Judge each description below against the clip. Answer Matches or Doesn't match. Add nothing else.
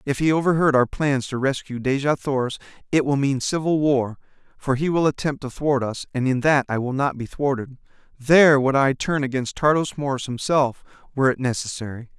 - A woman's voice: Doesn't match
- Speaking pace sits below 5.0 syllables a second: Doesn't match